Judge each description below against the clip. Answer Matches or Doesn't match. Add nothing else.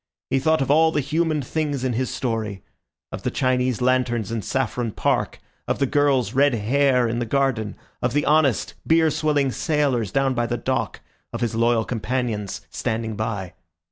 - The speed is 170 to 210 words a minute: Matches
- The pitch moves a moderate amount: Matches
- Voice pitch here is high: Doesn't match